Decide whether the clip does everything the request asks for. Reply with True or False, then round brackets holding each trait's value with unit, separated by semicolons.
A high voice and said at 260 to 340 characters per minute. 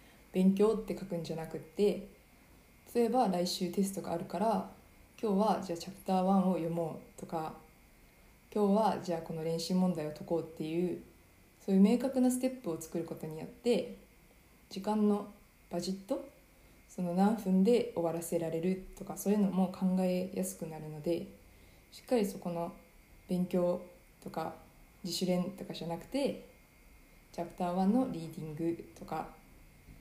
False (180 Hz; 310 characters per minute)